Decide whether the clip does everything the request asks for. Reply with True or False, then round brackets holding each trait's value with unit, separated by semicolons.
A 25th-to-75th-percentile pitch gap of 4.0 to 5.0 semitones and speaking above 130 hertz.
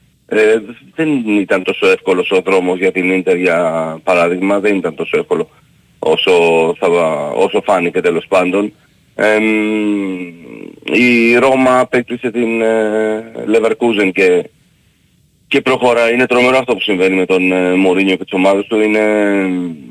False (4.5 semitones; 110 Hz)